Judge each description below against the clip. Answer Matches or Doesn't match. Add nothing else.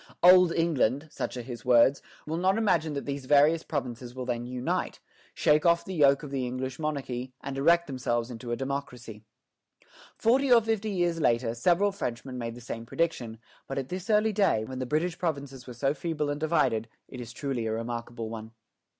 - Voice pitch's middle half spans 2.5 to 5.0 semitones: Doesn't match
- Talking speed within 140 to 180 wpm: Doesn't match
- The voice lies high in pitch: Doesn't match